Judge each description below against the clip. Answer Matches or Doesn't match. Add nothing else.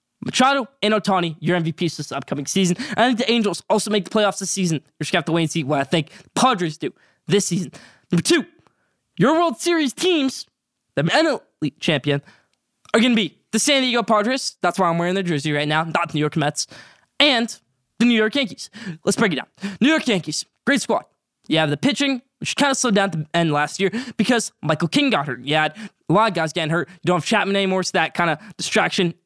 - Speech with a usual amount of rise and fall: Doesn't match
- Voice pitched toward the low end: Doesn't match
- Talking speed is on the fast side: Matches